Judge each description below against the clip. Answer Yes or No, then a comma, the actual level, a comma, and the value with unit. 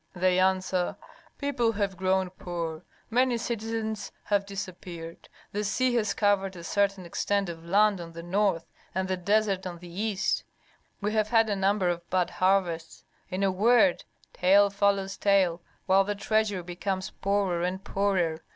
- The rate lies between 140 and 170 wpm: Yes, average, 160 wpm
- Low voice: No, high, 195 Hz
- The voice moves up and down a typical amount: No, narrow, 2.3 semitones